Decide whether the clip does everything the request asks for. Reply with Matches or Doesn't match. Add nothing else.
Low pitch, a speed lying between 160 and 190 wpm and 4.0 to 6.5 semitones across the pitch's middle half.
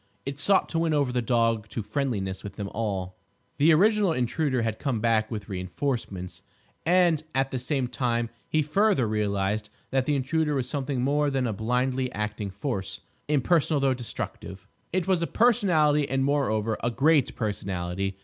Matches